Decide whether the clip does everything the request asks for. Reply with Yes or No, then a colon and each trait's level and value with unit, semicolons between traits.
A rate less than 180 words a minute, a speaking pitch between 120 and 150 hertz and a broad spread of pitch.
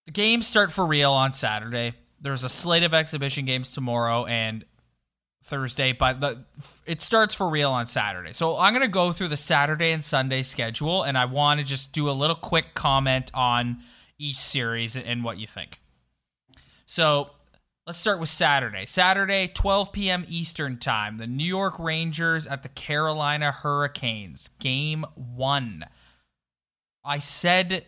No: average, 160 wpm; medium, 140 Hz; average, 4.8 semitones